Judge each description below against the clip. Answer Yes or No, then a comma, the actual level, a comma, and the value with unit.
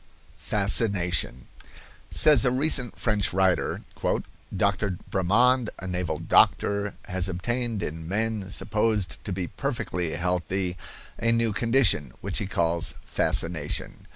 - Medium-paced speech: No, slow, 115 wpm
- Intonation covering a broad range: No, average, 4.3 semitones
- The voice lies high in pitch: No, low, 100 Hz